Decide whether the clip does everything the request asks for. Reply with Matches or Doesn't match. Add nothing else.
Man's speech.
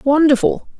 Doesn't match